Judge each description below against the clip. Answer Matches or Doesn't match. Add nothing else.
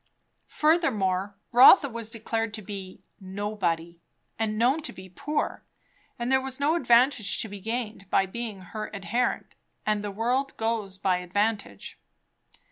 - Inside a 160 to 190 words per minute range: Doesn't match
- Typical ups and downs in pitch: Matches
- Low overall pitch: Doesn't match